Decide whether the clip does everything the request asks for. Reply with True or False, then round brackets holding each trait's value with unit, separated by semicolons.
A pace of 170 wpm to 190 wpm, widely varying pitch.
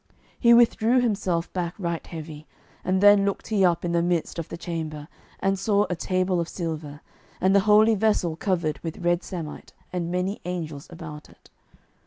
False (180 wpm; 3.0 semitones)